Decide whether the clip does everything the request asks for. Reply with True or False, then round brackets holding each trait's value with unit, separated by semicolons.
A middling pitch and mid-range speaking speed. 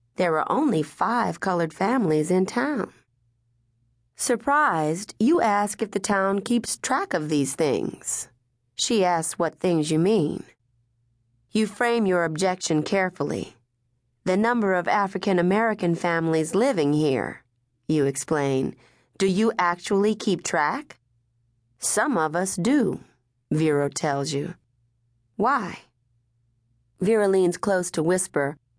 False (160 Hz; 120 wpm)